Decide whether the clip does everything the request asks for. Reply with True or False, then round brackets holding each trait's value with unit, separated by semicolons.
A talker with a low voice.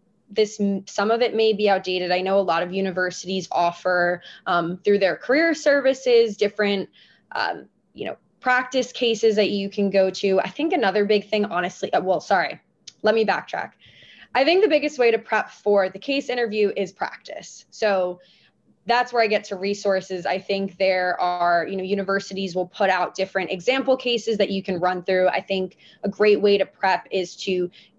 False (200 Hz)